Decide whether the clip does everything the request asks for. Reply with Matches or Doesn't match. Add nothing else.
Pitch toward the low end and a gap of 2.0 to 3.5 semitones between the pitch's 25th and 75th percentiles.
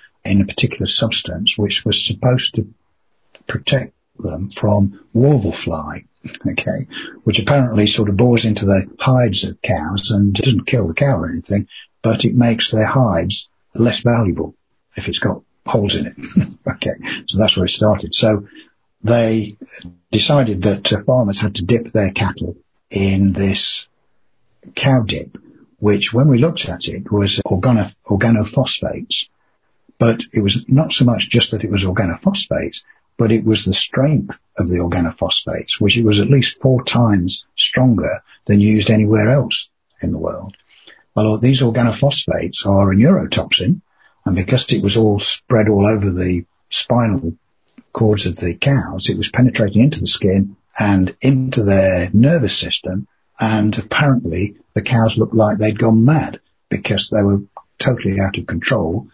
Matches